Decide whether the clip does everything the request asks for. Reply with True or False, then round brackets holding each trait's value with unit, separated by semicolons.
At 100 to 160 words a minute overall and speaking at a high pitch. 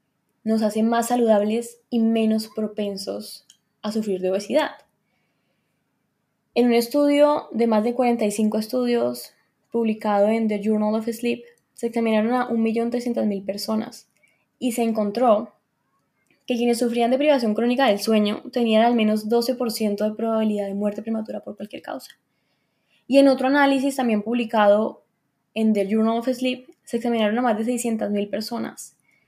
True (145 wpm; 225 Hz)